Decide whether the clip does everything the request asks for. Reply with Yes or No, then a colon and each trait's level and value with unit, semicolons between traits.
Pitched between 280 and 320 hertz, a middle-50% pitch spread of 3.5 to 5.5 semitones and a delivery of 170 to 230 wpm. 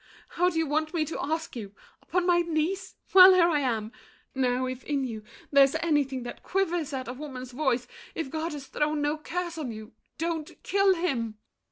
Yes: very high, 300 Hz; average, 4.6 semitones; average, 190 wpm